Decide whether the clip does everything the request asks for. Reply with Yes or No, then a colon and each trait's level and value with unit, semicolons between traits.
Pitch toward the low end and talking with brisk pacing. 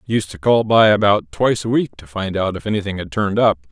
Yes: low, 100 Hz; fast, 260 wpm